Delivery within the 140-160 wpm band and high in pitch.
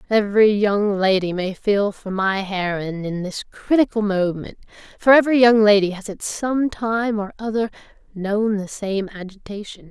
Yes: average, 155 wpm; high, 205 Hz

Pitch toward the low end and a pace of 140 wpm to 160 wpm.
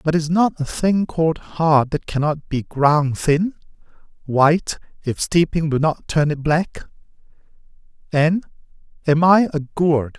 No: medium, 155 Hz; average, 145 wpm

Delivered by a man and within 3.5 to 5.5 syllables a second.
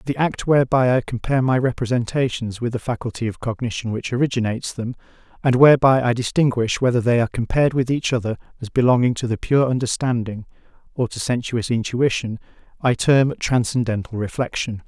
No: male; 6.0 syllables/s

